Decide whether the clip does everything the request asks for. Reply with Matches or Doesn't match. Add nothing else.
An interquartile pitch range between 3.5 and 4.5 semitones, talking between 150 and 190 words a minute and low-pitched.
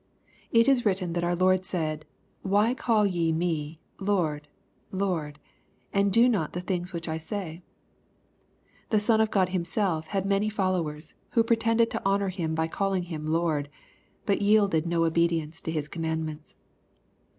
Doesn't match